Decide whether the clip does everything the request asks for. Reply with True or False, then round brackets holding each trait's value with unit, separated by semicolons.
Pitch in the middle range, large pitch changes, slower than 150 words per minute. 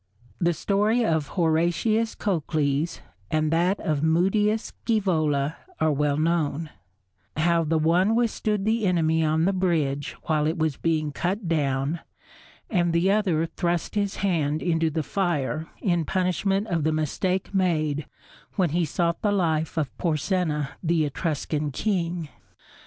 False (165 Hz; 3.3 semitones; 140 wpm)